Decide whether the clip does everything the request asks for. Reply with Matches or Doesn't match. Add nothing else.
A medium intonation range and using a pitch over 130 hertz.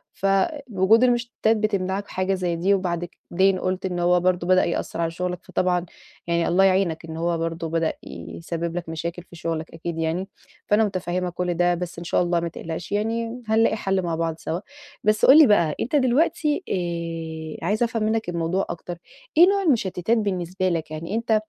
Matches